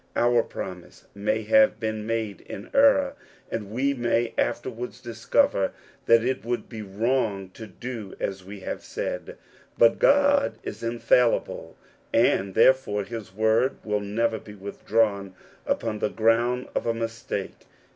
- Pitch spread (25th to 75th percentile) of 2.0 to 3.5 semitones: Yes, average, 2.8 semitones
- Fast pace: No, average, 140 wpm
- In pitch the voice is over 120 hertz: No, low, 115 Hz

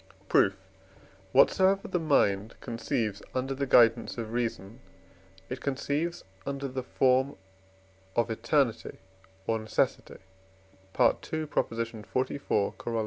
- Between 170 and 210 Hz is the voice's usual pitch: No, low, 125 Hz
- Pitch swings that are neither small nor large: Yes, average, 3.6 semitones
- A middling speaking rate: No, slow, 100 wpm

